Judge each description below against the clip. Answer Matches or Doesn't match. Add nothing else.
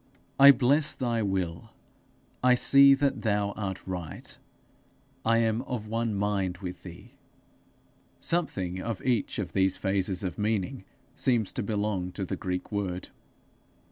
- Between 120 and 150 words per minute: Matches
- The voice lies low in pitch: Matches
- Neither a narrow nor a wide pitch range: Matches